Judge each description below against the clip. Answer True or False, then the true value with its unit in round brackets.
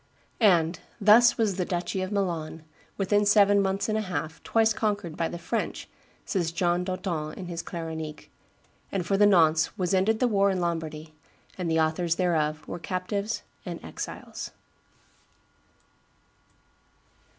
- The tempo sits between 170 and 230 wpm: False (145 wpm)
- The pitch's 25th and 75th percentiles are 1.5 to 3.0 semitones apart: False (3.6 semitones)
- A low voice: False (180 Hz)